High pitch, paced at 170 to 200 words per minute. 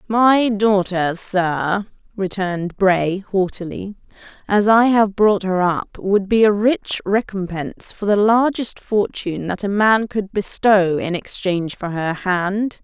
No: high, 195 Hz; average, 145 wpm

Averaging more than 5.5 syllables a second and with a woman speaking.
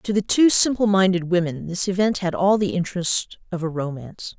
No: 5.4 syllables/s; female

